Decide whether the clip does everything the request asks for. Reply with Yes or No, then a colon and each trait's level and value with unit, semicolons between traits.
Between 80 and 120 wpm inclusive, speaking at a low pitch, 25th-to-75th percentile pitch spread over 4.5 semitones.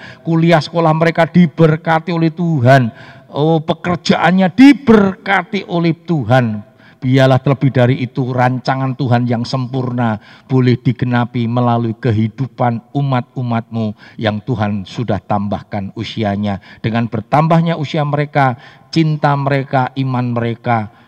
Yes: average, 105 wpm; low, 130 Hz; wide, 5.4 semitones